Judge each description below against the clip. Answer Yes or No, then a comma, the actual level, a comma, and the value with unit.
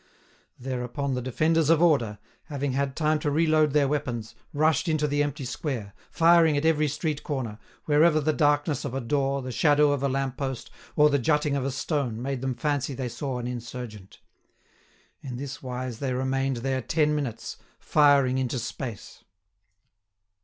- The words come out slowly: No, average, 170 wpm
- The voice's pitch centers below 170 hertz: Yes, medium, 140 Hz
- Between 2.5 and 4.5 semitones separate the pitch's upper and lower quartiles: Yes, average, 2.9 semitones